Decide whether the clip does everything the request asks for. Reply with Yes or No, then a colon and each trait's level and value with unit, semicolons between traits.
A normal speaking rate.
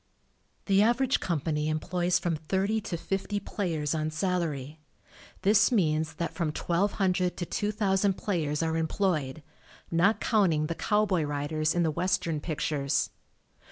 No: slow, 130 wpm